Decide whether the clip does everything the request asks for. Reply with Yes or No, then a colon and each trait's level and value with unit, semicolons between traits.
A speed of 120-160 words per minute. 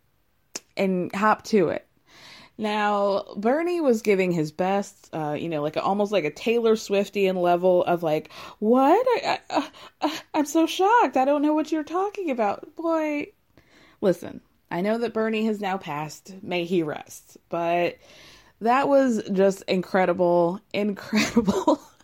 Yes: average, 145 wpm